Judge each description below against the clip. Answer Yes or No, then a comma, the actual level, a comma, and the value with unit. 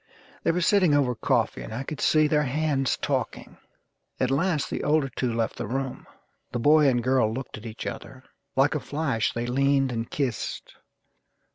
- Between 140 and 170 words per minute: No, average, 180 wpm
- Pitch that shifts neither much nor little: Yes, average, 3.5 semitones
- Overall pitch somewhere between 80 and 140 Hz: Yes, low, 135 Hz